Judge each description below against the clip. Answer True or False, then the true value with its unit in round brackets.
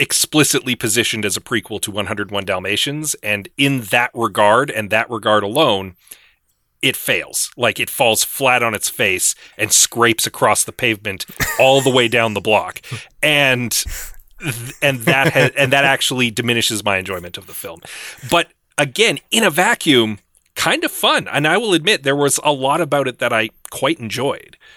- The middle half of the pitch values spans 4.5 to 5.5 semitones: True (4.8 semitones)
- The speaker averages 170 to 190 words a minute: True (175 wpm)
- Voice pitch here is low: True (120 Hz)